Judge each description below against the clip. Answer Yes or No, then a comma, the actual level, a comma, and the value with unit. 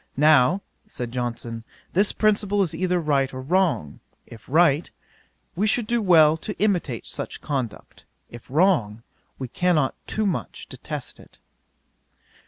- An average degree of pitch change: No, wide, 6.9 semitones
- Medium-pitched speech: Yes, medium, 155 Hz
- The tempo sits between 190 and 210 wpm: No, slow, 135 wpm